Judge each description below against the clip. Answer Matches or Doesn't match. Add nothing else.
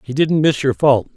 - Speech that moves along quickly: Matches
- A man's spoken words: Matches